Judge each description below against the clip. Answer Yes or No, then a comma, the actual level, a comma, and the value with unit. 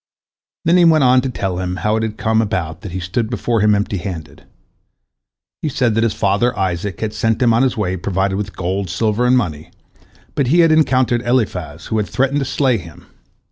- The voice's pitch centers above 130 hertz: No, low, 110 Hz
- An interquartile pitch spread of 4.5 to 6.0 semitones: Yes, average, 4.9 semitones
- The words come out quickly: Yes, fast, 220 wpm